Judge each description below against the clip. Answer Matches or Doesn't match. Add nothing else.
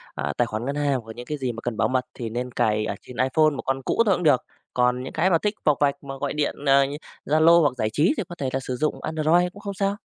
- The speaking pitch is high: Doesn't match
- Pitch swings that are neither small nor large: Matches